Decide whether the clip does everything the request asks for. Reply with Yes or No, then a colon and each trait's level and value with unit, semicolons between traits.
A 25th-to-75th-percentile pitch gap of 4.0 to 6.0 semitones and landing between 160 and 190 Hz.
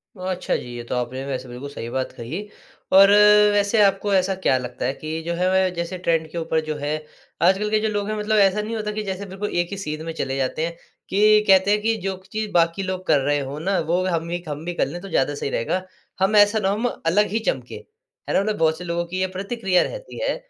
Yes: average, 4.5 semitones; medium, 185 Hz